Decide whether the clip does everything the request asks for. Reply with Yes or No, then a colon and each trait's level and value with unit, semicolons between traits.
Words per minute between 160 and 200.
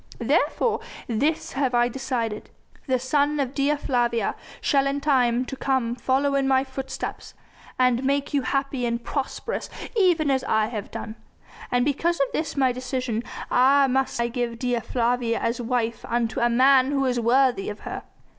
Yes: average, 165 wpm